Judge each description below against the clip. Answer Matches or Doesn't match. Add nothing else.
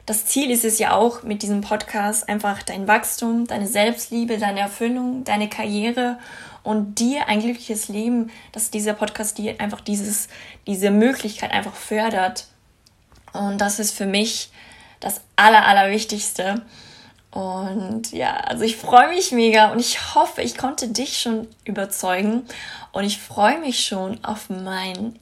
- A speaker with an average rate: Matches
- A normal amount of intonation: Doesn't match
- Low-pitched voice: Doesn't match